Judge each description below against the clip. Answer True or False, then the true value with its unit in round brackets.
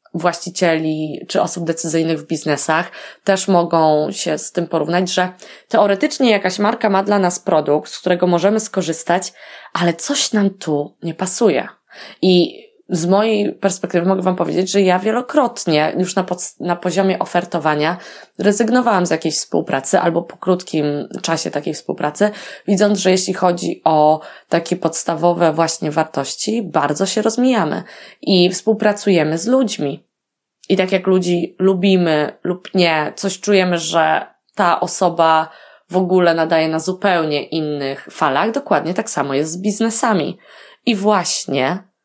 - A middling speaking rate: True (140 wpm)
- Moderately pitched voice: True (180 Hz)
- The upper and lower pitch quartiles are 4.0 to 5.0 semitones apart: False (3.4 semitones)